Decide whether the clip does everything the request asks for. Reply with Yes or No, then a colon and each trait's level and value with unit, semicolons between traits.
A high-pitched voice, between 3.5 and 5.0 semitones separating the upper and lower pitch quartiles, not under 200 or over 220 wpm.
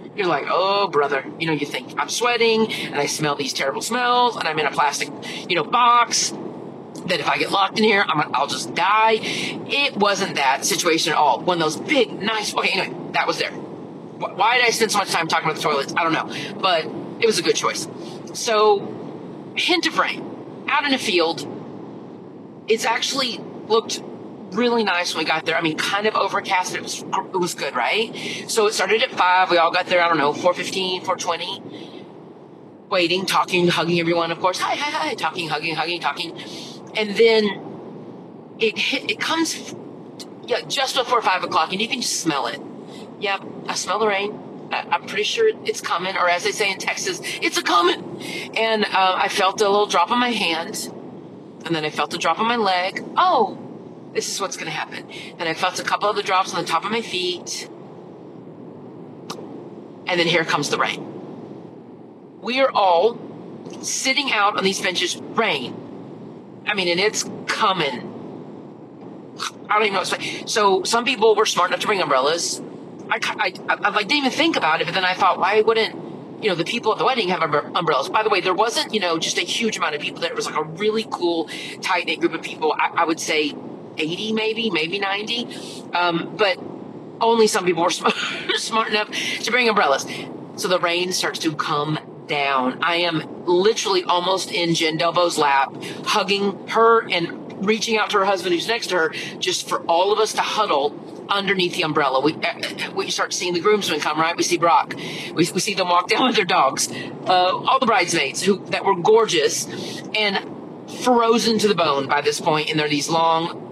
Yes: high, 195 Hz; average, 4.6 semitones; fast, 205 wpm